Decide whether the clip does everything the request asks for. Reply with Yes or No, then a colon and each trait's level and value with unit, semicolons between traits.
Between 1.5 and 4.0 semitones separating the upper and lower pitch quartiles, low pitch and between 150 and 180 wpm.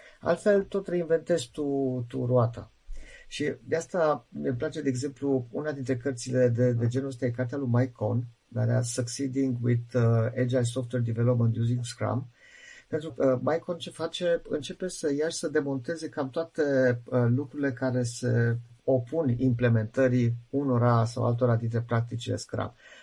Yes: average, 3.4 semitones; low, 130 Hz; average, 160 wpm